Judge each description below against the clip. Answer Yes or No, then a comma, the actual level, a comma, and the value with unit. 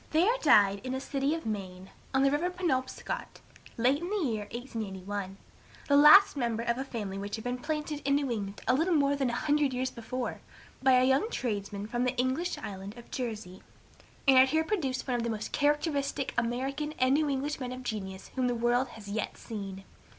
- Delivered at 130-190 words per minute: No, fast, 205 wpm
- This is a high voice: Yes, very high, 255 Hz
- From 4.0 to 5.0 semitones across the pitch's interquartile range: Yes, average, 4.5 semitones